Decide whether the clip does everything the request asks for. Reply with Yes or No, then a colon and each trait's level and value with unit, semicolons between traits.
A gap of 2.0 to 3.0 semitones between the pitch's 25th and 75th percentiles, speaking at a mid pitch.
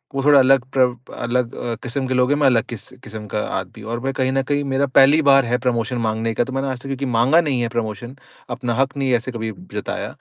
No: narrow, 2.6 semitones; low, 125 Hz